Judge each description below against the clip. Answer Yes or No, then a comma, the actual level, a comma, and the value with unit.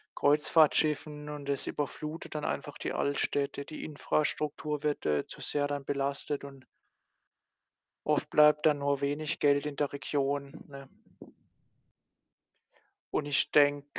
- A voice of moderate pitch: Yes, medium, 145 Hz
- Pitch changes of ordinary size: No, narrow, 1.0 semitones